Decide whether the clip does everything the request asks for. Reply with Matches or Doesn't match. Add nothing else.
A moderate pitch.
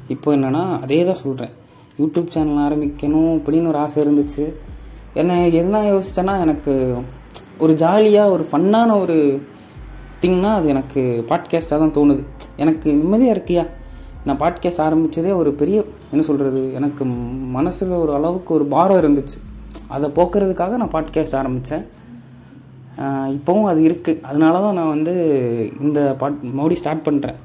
Matches